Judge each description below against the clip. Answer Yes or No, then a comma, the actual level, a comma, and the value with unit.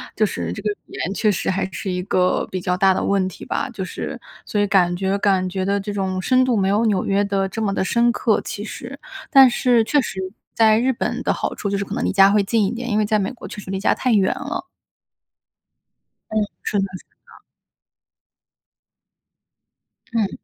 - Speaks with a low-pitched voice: No, high, 200 Hz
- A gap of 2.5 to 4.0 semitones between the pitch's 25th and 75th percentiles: Yes, average, 2.8 semitones